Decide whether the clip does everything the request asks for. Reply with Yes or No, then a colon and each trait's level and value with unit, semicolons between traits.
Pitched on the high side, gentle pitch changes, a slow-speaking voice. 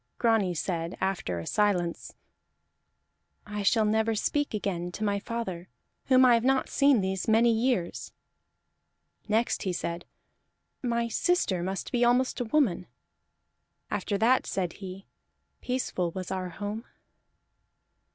No: high, 210 Hz; average, 4.3 semitones; slow, 130 wpm